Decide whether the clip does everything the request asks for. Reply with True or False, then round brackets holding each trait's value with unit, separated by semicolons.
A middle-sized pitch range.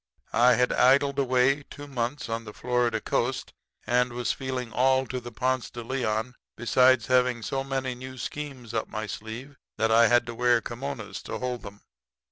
False (1.9 semitones)